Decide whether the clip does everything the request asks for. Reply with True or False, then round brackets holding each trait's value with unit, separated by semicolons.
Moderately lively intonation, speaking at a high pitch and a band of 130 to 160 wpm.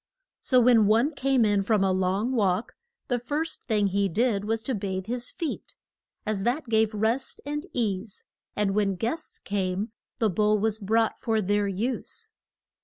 False (3.5 semitones; 220 Hz; 170 wpm)